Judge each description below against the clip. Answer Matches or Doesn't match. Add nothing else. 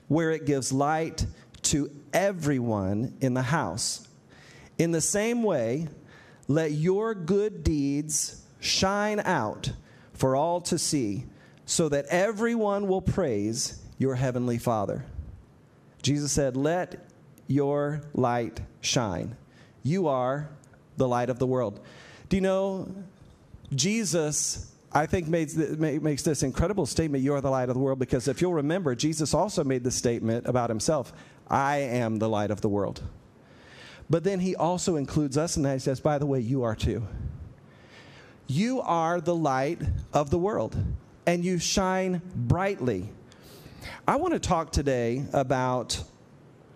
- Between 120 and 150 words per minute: Matches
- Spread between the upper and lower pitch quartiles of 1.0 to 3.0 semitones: Doesn't match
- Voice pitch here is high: Doesn't match